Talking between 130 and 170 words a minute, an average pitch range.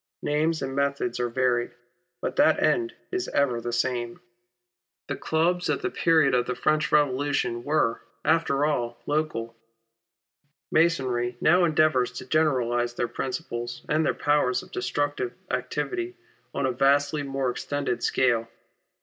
Yes: average, 140 wpm; average, 3.9 semitones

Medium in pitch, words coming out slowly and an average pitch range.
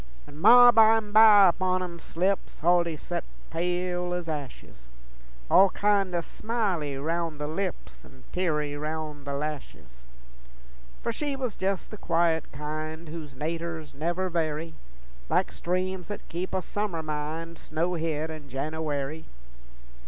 Yes: medium, 165 Hz; slow, 130 wpm; average, 3.5 semitones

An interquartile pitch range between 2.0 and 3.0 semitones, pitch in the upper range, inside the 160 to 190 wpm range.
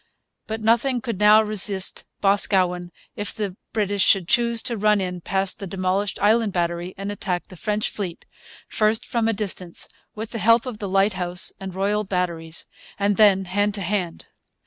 Yes: narrow, 2.6 semitones; high, 200 Hz; average, 170 wpm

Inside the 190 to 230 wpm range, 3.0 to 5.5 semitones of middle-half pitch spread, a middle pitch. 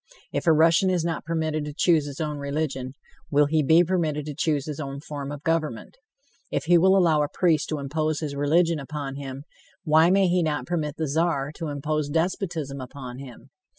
No: average, 200 wpm; narrow, 2.6 semitones; medium, 155 Hz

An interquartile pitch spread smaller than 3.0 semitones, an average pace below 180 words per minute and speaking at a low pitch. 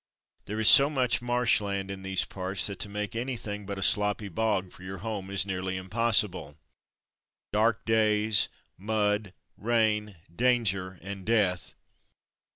Yes: narrow, 2.6 semitones; average, 150 wpm; low, 105 Hz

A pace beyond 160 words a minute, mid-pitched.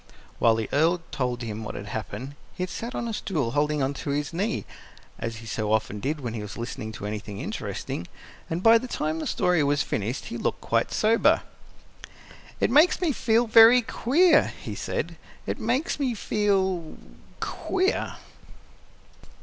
Yes: average, 175 wpm; medium, 150 Hz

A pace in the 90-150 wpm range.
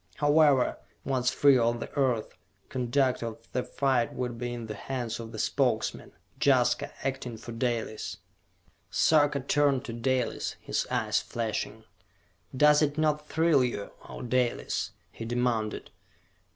Yes: average, 140 wpm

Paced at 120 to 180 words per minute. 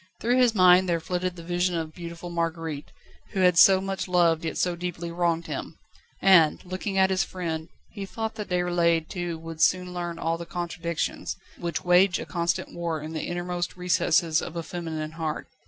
No: average, 190 wpm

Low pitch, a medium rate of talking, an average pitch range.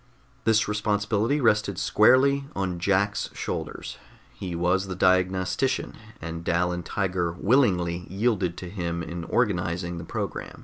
No: very low, 95 Hz; slow, 130 wpm; average, 3.2 semitones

